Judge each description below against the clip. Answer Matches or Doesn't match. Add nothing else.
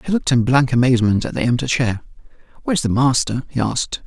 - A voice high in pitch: Doesn't match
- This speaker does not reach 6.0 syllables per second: Doesn't match